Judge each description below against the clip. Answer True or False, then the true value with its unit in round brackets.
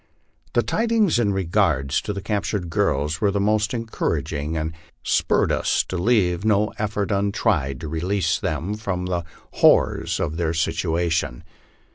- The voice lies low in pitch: True (90 Hz)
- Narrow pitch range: False (4.4 semitones)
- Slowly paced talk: False (150 wpm)